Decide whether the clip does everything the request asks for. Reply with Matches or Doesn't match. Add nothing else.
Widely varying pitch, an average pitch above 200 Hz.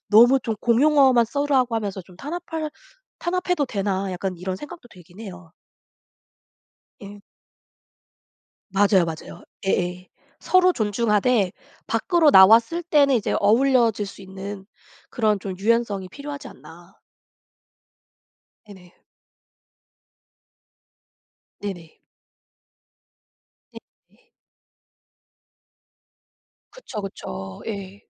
Matches